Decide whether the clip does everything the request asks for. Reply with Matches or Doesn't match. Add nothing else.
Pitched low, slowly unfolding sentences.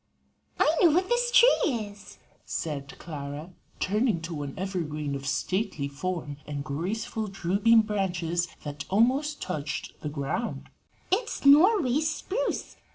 Doesn't match